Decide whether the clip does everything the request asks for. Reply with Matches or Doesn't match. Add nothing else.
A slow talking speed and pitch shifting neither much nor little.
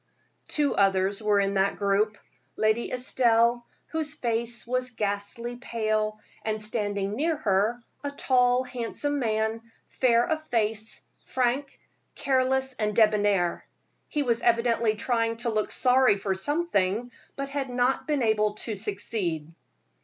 Matches